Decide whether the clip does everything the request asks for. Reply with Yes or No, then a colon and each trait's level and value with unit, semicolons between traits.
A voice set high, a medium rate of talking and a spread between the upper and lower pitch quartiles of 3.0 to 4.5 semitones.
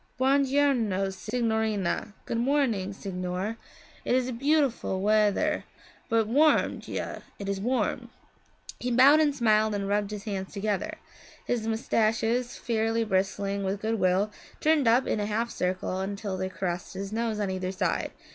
Yes: high, 215 Hz; average, 155 wpm; average, 3.7 semitones